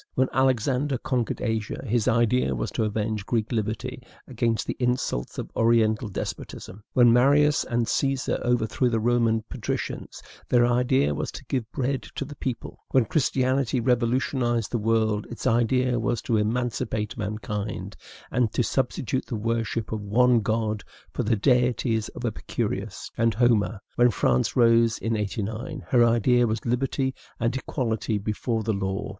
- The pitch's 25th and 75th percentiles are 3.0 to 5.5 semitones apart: No, narrow, 2.4 semitones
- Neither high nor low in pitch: No, low, 115 Hz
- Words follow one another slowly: No, average, 150 wpm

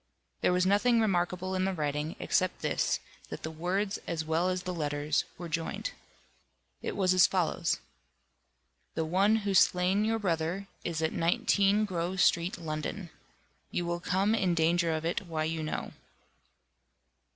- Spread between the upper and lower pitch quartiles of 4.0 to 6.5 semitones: No, average, 2.9 semitones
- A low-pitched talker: No, medium, 175 Hz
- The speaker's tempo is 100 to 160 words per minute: Yes, average, 155 wpm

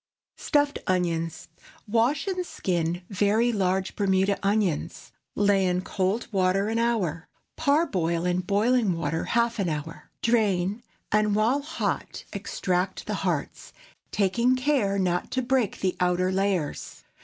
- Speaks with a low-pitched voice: No, high, 200 Hz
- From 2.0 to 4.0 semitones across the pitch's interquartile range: No, average, 4.5 semitones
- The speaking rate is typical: No, slow, 130 wpm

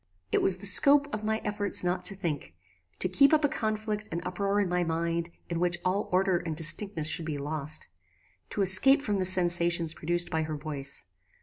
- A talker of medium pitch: Yes, medium, 180 Hz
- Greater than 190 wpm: Yes, average, 200 wpm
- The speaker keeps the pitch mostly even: No, average, 3.7 semitones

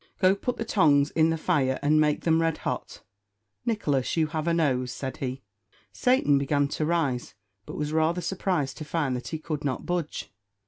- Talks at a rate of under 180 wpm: No, average, 190 wpm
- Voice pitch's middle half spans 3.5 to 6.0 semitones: No, average, 3.1 semitones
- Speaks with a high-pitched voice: No, medium, 155 Hz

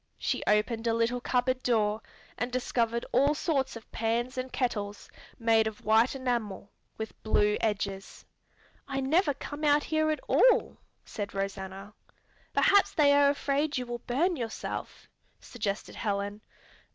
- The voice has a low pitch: No, high, 240 Hz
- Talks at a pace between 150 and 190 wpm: No, average, 140 wpm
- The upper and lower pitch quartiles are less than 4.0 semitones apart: No, average, 4.4 semitones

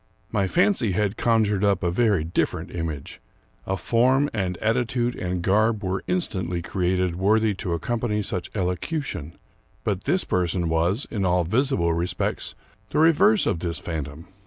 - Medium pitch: No, very low, 95 Hz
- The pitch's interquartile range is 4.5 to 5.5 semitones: Yes, average, 4.9 semitones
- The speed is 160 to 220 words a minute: No, average, 150 wpm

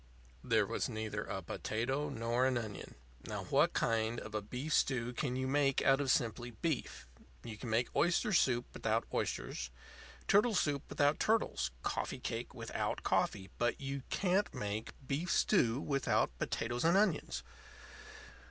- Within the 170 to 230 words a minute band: No, average, 150 wpm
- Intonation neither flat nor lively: Yes, average, 4.3 semitones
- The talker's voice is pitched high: No, low, 130 Hz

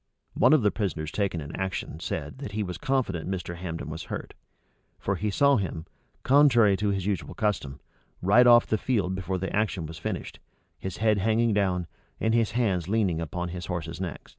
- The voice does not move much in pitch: No, average, 3.9 semitones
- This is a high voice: No, very low, 95 Hz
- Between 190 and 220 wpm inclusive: Yes, average, 195 wpm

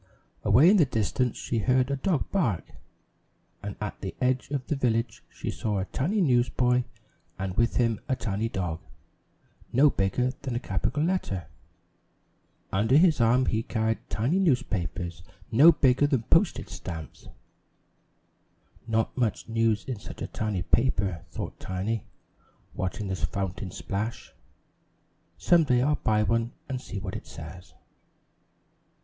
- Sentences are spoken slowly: No, average, 145 wpm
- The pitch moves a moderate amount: Yes, average, 4.8 semitones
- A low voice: Yes, low, 115 Hz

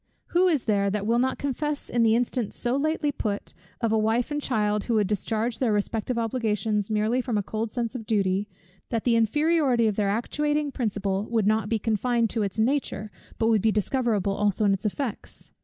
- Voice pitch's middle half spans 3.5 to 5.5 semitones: No, average, 3.0 semitones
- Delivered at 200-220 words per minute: Yes, fast, 205 wpm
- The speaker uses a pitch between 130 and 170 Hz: No, high, 225 Hz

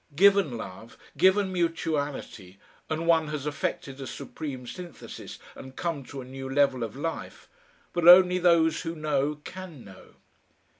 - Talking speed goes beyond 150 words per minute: No, average, 145 wpm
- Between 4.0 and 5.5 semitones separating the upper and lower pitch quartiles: Yes, average, 4.4 semitones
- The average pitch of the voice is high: No, medium, 150 Hz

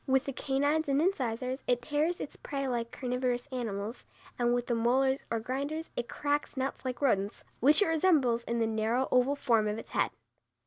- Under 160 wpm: No, average, 190 wpm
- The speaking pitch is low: No, very high, 255 Hz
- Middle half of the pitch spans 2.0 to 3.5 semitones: Yes, average, 3.2 semitones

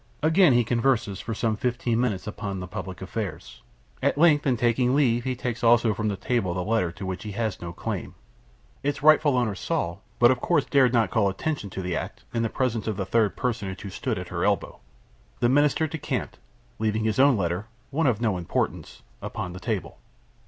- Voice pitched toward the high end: No, low, 115 Hz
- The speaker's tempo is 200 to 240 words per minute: Yes, fast, 205 wpm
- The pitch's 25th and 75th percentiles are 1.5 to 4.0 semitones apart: No, average, 4.4 semitones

